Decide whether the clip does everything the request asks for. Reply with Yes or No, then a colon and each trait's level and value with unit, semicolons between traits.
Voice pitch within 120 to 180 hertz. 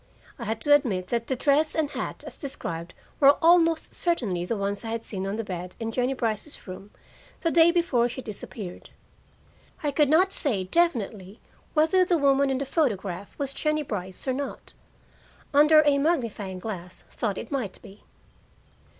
No: very high, 250 Hz